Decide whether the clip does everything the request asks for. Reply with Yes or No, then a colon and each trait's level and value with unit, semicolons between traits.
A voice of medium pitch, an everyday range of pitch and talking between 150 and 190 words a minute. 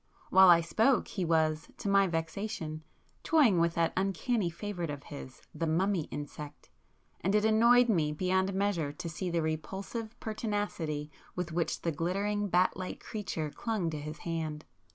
Yes: medium, 175 Hz; average, 4.4 semitones; average, 155 wpm